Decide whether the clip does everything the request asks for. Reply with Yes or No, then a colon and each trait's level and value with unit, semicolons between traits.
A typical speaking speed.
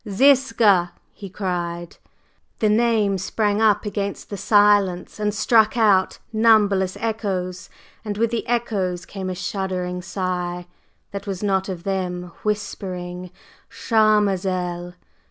No: slow, 120 wpm